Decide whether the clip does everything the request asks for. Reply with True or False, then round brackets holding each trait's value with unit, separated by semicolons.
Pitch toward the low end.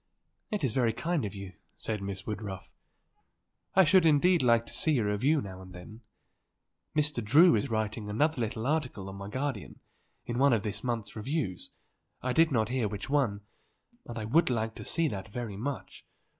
True (115 Hz)